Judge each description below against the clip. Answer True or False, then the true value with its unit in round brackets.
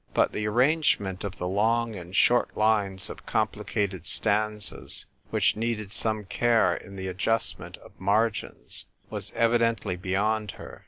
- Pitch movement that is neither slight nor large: True (3.0 semitones)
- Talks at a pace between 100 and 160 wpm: True (140 wpm)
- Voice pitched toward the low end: True (105 Hz)